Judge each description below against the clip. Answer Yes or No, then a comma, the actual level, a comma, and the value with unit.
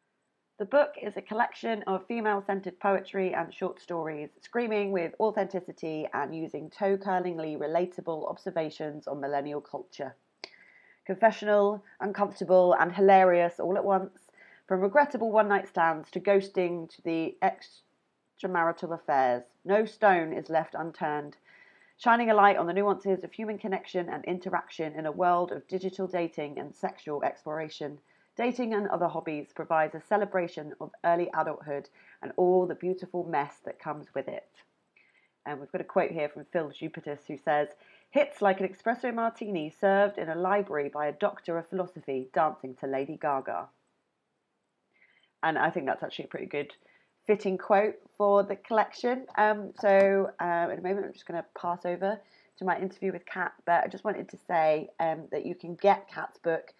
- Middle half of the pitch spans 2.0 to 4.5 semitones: Yes, average, 3.9 semitones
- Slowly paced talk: No, average, 165 wpm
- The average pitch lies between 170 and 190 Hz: Yes, medium, 185 Hz